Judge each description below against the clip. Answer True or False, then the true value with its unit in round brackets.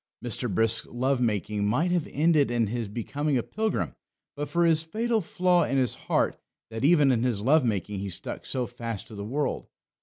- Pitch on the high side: False (125 Hz)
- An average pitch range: False (5.8 semitones)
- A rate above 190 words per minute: True (200 wpm)